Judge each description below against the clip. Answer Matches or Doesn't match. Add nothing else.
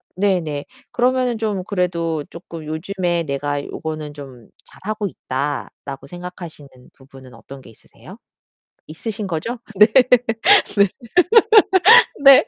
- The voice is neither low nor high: Matches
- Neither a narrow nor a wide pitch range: Doesn't match